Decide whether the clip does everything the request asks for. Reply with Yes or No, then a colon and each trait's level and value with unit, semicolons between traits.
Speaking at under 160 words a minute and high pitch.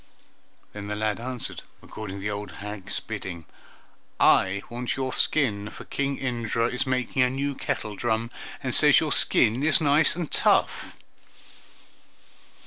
No: average, 140 wpm; low, 115 Hz